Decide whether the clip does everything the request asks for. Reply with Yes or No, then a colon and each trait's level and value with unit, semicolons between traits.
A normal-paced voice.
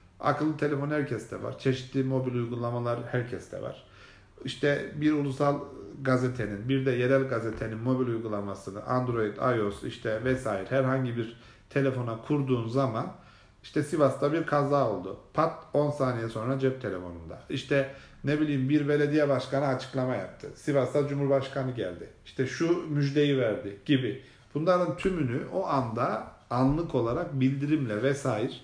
Yes: average, 130 wpm